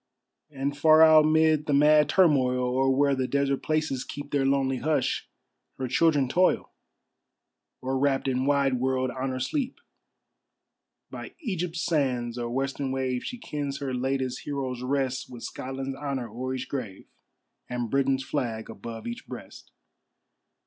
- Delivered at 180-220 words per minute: No, average, 145 wpm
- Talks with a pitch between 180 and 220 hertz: No, low, 135 Hz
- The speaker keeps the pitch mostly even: Yes, narrow, 2.2 semitones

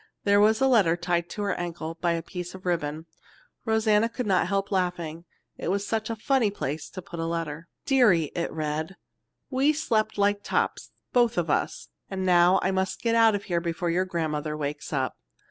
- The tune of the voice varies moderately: Yes, average, 4.2 semitones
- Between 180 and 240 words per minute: Yes, average, 195 wpm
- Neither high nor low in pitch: Yes, medium, 180 Hz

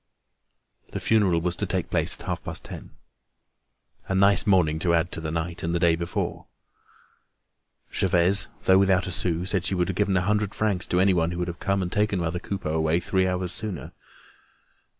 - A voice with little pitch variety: Yes, narrow, 2.2 semitones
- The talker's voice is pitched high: No, very low, 90 Hz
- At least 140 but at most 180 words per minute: No, average, 195 wpm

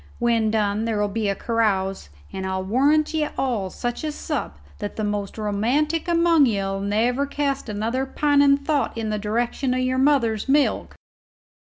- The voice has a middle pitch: No, high, 230 Hz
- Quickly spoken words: No, average, 165 wpm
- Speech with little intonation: No, average, 5.2 semitones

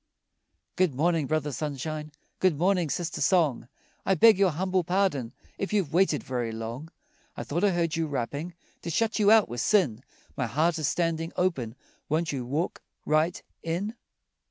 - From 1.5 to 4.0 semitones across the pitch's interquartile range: No, average, 4.4 semitones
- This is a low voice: No, medium, 160 Hz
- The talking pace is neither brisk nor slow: Yes, average, 165 wpm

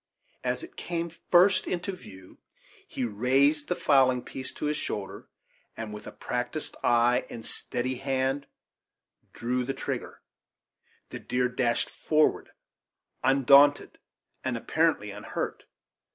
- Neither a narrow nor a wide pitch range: Yes, average, 3.5 semitones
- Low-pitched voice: Yes, low, 130 Hz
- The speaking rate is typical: No, slow, 125 wpm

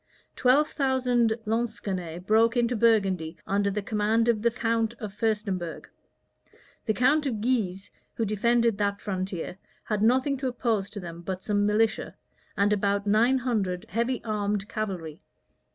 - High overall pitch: Yes, high, 215 Hz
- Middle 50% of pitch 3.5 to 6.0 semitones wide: No, average, 2.9 semitones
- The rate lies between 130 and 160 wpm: Yes, average, 145 wpm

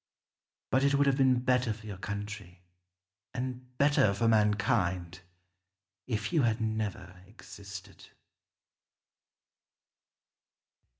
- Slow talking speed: Yes, slow, 100 wpm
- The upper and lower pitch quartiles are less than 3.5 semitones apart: No, average, 4.1 semitones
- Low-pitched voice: Yes, low, 110 Hz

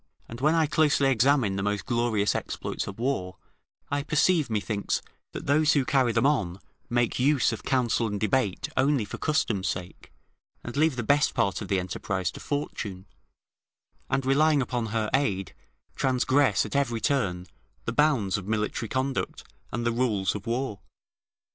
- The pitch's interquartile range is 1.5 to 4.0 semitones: No, average, 5.3 semitones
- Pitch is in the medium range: No, low, 120 Hz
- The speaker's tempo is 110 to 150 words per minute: No, average, 165 wpm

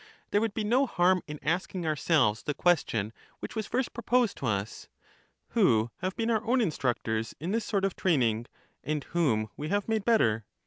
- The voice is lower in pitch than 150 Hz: No, medium, 175 Hz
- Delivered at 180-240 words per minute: Yes, average, 190 wpm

